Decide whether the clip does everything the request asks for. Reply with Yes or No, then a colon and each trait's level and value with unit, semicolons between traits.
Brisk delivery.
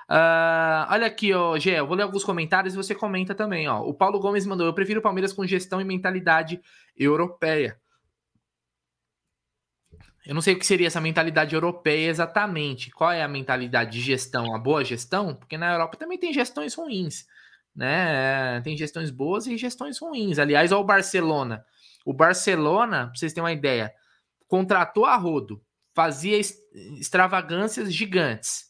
No: average, 160 wpm